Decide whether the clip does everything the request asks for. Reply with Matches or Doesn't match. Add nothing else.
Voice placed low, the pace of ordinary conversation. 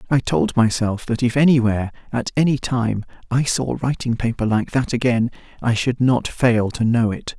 Matches